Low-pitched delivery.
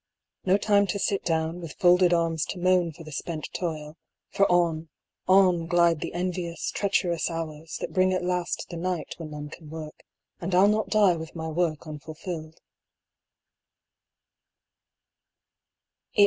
No: medium, 170 Hz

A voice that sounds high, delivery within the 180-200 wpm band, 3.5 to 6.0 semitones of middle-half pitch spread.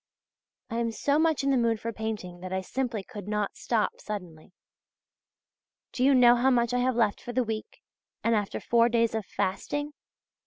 No: high, 230 Hz; average, 190 wpm; average, 3.0 semitones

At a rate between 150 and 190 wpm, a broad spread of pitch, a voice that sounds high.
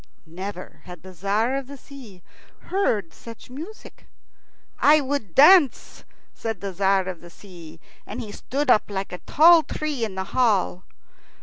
Yes: average, 160 wpm; wide, 6.7 semitones; high, 215 Hz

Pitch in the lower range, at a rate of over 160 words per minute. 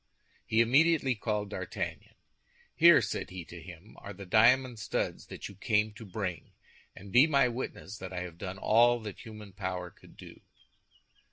Yes: low, 105 Hz; average, 170 wpm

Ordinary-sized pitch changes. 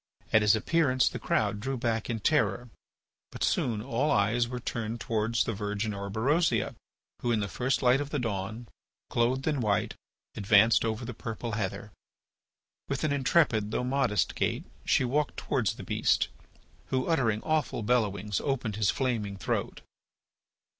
Yes: average, 3.5 semitones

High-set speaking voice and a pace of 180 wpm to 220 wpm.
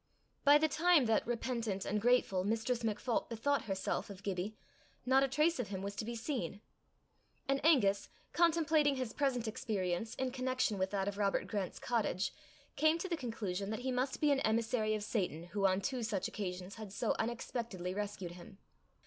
Yes: high, 225 Hz; average, 185 wpm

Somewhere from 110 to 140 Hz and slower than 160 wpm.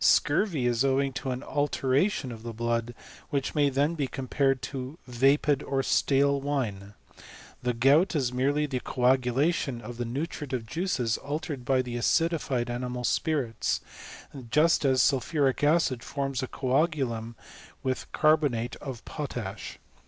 Yes: low, 135 Hz; slow, 135 wpm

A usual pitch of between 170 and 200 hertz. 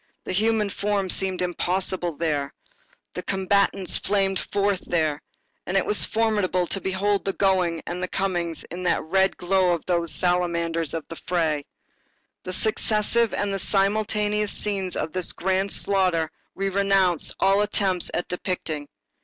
Yes: medium, 185 Hz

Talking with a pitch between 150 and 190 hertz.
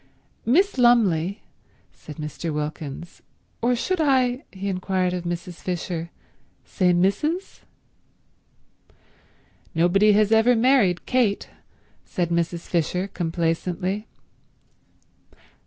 Yes: medium, 185 Hz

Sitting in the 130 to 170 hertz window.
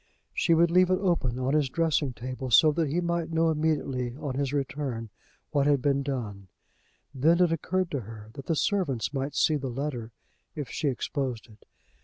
Yes: medium, 140 Hz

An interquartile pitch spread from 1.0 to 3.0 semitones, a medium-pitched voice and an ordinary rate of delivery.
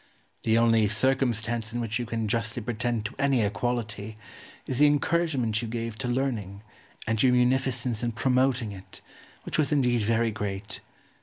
No: narrow, 2.6 semitones; low, 115 Hz; average, 160 wpm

